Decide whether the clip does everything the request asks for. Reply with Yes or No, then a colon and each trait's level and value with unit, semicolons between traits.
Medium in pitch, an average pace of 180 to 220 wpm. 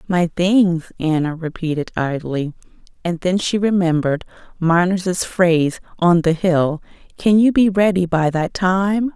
No: medium, 175 Hz; average, 140 wpm